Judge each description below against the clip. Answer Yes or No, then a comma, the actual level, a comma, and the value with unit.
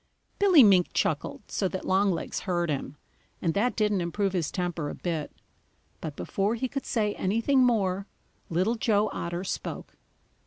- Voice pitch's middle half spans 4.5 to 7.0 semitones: No, average, 4.1 semitones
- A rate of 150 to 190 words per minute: Yes, average, 155 wpm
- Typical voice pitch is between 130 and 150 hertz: No, high, 195 Hz